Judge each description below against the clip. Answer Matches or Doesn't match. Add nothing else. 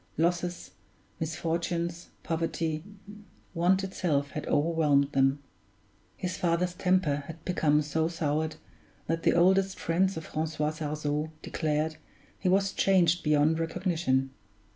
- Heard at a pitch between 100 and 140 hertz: Doesn't match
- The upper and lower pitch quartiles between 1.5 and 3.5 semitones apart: Matches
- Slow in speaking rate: Matches